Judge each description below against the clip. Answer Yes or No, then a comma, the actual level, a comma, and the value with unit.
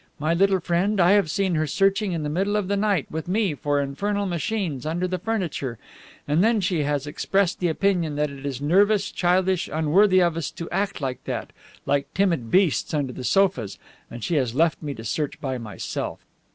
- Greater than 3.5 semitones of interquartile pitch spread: Yes, average, 5.2 semitones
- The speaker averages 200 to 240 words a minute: Yes, fast, 205 wpm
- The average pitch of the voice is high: No, medium, 170 Hz